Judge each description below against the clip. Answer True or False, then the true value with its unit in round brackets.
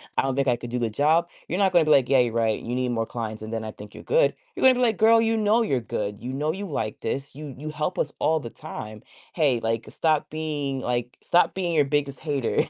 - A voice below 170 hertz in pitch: True (140 Hz)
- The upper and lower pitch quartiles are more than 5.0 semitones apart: True (5.6 semitones)